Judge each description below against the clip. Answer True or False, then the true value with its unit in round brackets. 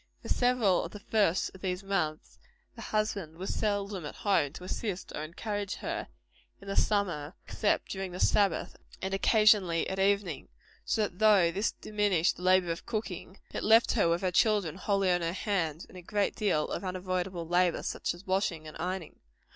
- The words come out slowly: False (185 wpm)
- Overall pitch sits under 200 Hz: True (190 Hz)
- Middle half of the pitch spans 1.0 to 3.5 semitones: True (2.7 semitones)